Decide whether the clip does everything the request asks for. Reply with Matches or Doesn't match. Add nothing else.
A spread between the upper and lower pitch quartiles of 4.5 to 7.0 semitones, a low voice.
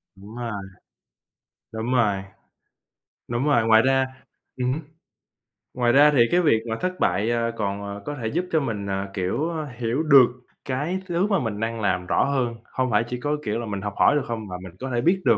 Matches